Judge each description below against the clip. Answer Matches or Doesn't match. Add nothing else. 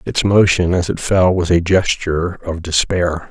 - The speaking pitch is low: Matches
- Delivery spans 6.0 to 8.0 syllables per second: Doesn't match